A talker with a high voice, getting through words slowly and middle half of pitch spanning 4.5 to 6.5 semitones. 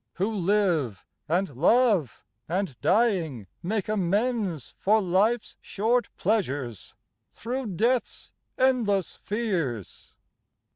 Yes: high, 195 Hz; slow, 90 wpm; average, 5.1 semitones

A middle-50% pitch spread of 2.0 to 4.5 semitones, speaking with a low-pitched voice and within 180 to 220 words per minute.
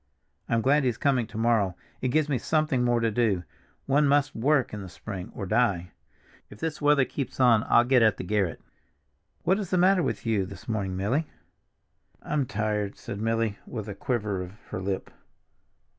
No: average, 5.2 semitones; low, 115 Hz; average, 190 wpm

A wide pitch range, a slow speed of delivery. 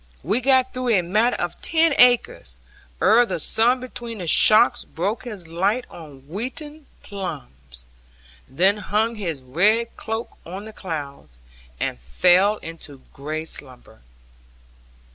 Yes: wide, 7.2 semitones; slow, 130 wpm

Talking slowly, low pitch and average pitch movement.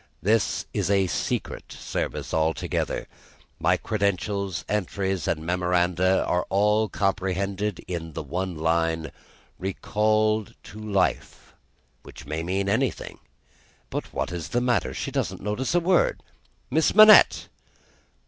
Yes: slow, 120 wpm; very low, 95 Hz; average, 3.2 semitones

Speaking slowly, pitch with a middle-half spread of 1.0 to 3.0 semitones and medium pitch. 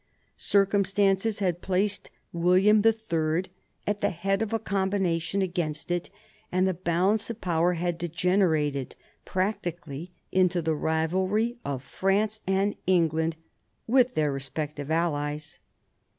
No: slow, 120 wpm; average, 3.6 semitones; medium, 180 Hz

